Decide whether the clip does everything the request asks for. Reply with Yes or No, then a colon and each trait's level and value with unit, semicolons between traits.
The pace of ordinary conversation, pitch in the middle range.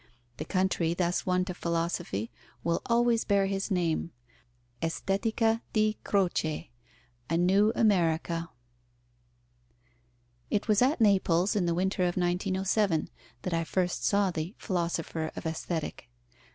No: slow, 125 wpm; medium, 180 Hz